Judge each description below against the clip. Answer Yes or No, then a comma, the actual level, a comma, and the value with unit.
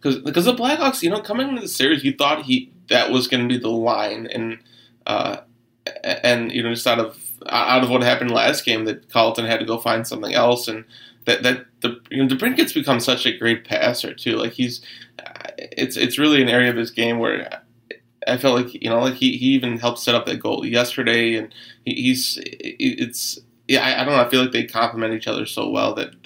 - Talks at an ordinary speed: No, fast, 230 wpm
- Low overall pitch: Yes, low, 120 Hz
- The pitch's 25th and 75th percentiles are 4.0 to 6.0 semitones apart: Yes, average, 4.4 semitones